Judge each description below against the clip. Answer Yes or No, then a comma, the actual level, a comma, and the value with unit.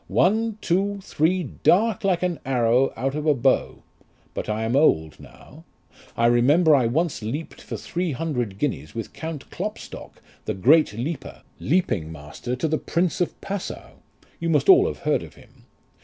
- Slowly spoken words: No, average, 170 wpm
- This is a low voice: No, medium, 150 Hz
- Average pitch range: No, wide, 6.7 semitones